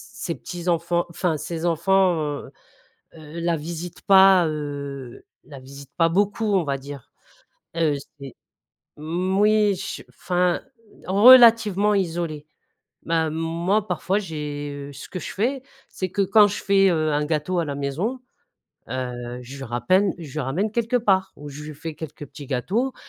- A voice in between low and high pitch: Yes, medium, 170 Hz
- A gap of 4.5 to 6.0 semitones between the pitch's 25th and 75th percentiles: Yes, average, 4.8 semitones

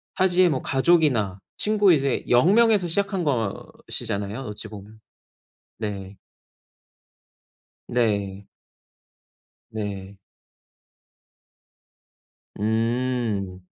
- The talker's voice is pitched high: No, low, 115 Hz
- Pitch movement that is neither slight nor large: No, wide, 8.1 semitones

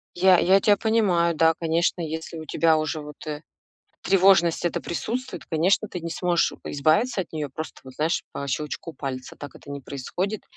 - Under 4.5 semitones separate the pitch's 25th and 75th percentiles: Yes, average, 3.5 semitones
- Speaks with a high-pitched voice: No, medium, 165 Hz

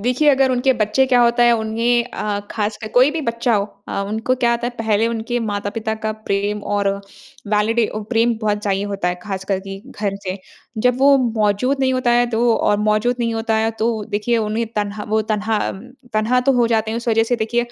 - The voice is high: Yes, high, 225 Hz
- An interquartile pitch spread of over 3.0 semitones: No, narrow, 2.4 semitones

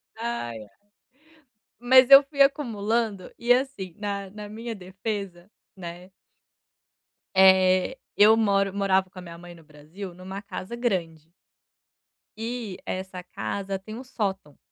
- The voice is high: Yes, high, 195 Hz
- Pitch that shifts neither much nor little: Yes, average, 3.7 semitones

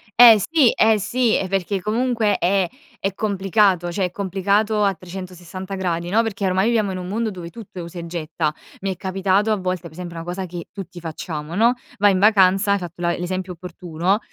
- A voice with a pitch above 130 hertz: Yes, high, 190 Hz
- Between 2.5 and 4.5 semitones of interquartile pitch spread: Yes, average, 2.8 semitones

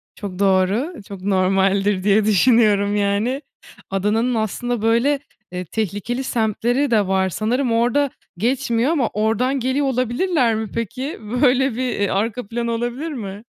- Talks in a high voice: Yes, high, 225 Hz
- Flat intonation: No, average, 3.8 semitones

